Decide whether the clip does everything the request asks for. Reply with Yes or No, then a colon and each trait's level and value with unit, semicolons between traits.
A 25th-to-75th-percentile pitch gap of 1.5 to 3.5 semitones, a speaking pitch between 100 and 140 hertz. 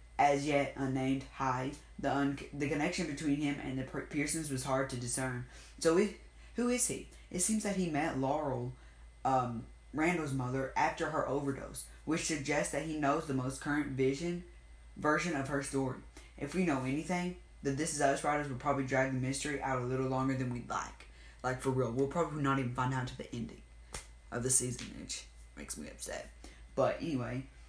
Yes: narrow, 2.5 semitones; low, 135 Hz